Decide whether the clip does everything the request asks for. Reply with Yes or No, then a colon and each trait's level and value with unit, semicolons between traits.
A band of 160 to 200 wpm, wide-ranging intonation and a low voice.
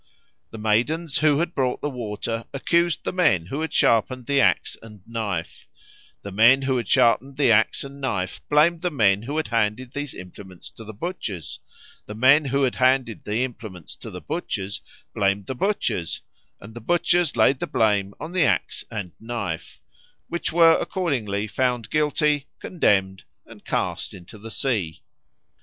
Yes: average, 170 wpm; wide, 5.7 semitones; low, 120 Hz